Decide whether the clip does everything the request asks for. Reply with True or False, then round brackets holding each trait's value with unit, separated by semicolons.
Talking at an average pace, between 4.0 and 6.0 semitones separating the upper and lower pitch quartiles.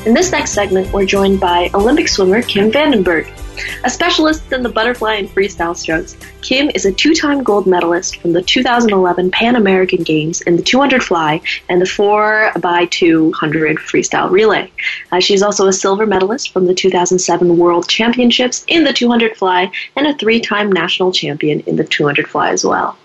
True (175 wpm; 5.1 semitones)